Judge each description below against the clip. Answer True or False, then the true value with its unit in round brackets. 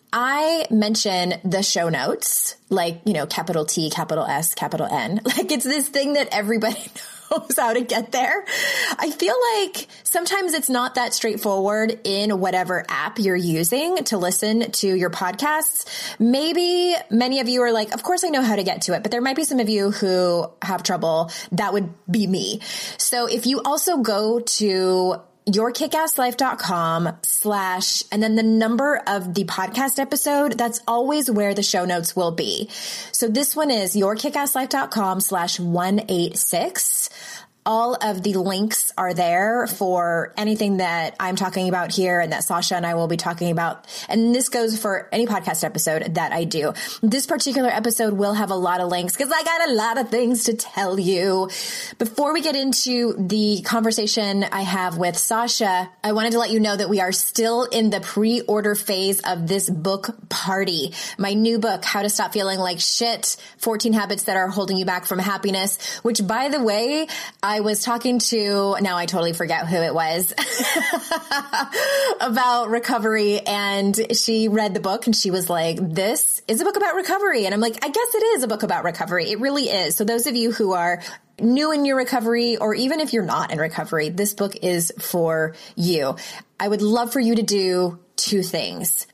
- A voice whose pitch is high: True (215 Hz)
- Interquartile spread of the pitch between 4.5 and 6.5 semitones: True (4.8 semitones)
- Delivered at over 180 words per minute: True (190 wpm)